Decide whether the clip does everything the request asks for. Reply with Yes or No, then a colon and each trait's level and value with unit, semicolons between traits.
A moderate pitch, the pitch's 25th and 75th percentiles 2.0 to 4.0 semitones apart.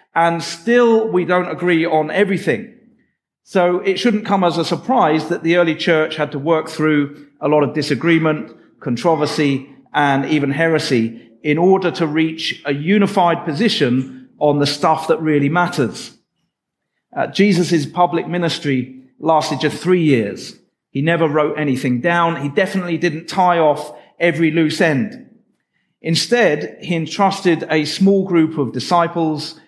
Yes: medium, 165 Hz; average, 3.0 semitones